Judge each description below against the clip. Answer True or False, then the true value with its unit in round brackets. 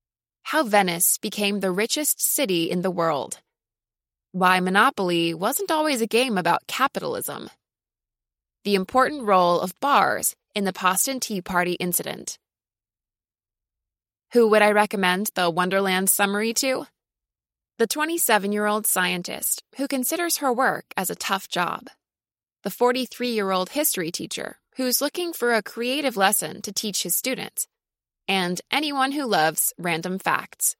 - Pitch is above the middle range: True (205 Hz)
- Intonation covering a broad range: True (6.0 semitones)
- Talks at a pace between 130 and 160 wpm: True (140 wpm)